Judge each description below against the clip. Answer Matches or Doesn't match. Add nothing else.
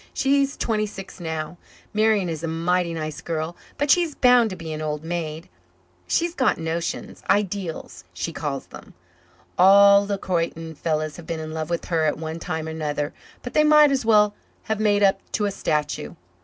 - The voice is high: Doesn't match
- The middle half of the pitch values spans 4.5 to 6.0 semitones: Matches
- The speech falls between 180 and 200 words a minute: Matches